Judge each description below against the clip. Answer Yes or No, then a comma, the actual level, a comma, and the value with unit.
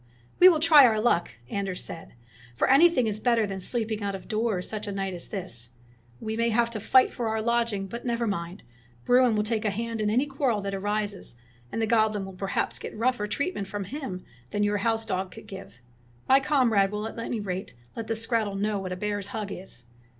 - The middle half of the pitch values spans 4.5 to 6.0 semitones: No, average, 3.0 semitones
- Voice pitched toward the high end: Yes, high, 215 Hz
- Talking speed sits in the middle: No, fast, 220 wpm